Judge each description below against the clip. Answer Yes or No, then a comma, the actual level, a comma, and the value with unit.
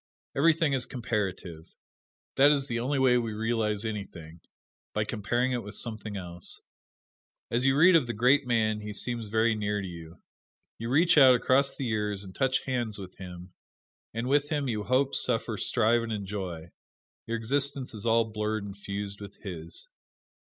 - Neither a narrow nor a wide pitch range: Yes, average, 4.0 semitones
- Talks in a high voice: No, low, 110 Hz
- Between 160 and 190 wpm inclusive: Yes, average, 170 wpm